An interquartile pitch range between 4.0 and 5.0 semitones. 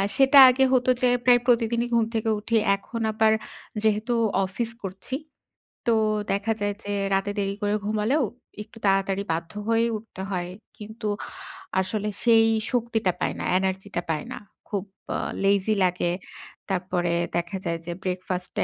No: average, 3.2 semitones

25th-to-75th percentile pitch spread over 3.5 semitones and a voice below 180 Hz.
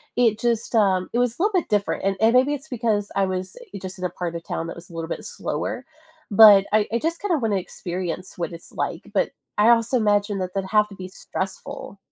No: average, 4.2 semitones; high, 205 Hz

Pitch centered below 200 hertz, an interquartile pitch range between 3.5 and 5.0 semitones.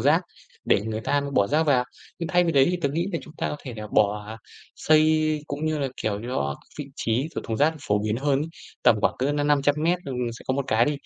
No: medium, 140 Hz; wide, 5.6 semitones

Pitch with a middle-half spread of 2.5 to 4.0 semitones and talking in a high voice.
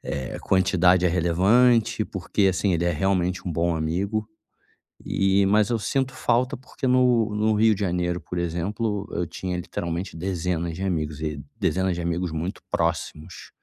No: average, 3.6 semitones; very low, 95 Hz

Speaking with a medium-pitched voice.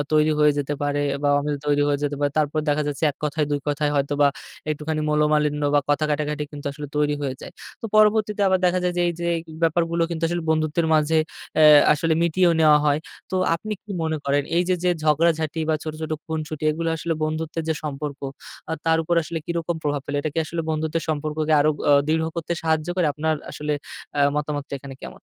Yes: medium, 155 Hz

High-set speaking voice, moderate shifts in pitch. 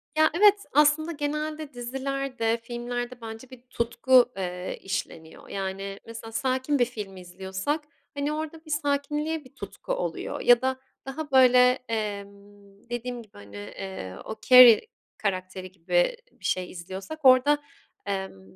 No: high, 245 Hz; wide, 6.4 semitones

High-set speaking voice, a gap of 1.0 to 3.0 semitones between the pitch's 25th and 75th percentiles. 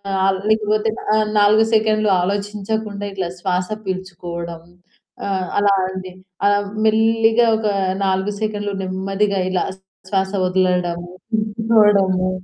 Yes: high, 200 Hz; narrow, 2.4 semitones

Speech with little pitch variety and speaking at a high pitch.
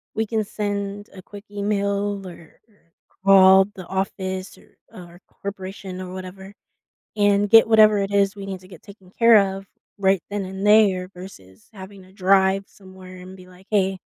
Yes: narrow, 1.4 semitones; high, 195 Hz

